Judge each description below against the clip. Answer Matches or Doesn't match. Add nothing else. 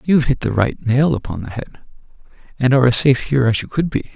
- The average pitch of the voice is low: Matches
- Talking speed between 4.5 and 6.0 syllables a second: Doesn't match